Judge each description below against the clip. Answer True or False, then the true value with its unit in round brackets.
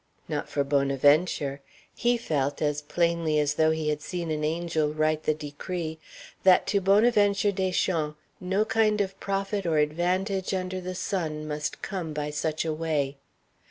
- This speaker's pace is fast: False (160 wpm)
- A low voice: False (160 Hz)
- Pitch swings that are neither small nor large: True (4.0 semitones)